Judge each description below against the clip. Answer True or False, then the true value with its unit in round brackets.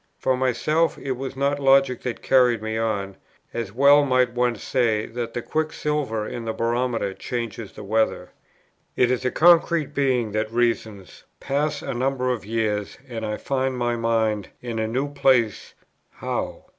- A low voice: True (120 Hz)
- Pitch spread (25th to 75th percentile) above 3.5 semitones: False (3.2 semitones)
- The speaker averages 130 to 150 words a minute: False (165 wpm)